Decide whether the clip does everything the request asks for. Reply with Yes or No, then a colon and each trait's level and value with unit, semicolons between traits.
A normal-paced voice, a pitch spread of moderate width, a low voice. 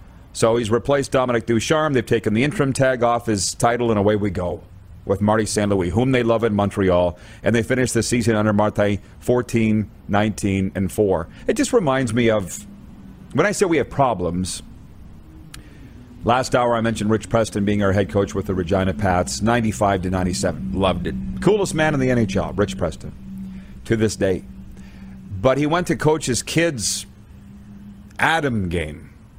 Yes: average, 175 wpm; average, 3.7 semitones; low, 105 Hz